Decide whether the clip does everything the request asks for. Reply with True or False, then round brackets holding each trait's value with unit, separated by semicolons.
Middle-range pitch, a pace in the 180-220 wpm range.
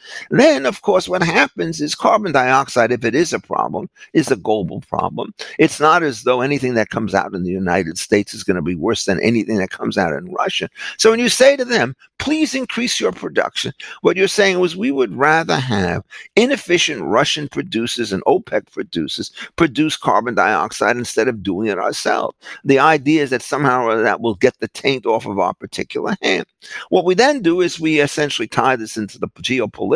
True (155 Hz; 200 wpm)